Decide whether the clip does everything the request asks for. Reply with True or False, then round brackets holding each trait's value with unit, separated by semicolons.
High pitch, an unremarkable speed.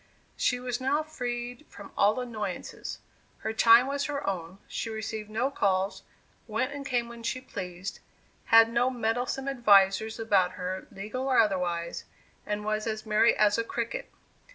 True (225 Hz; 155 wpm)